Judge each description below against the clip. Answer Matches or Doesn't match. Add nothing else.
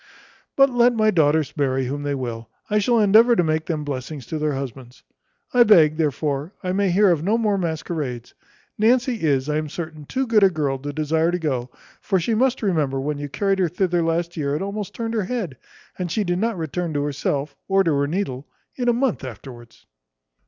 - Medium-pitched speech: Matches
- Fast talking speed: Matches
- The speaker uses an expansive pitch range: Matches